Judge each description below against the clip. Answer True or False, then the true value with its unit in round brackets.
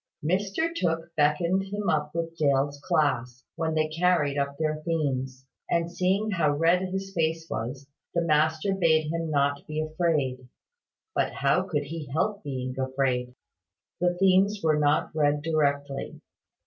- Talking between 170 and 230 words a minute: False (150 wpm)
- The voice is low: False (155 Hz)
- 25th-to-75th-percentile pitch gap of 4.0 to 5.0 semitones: False (3.3 semitones)